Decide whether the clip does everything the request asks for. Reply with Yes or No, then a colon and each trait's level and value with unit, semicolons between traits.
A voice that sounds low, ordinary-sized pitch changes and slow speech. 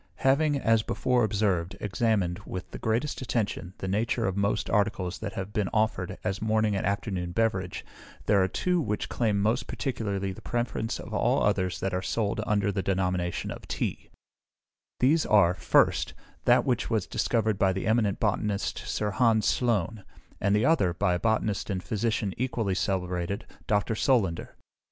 No: low, 105 Hz; average, 3.0 semitones; average, 165 wpm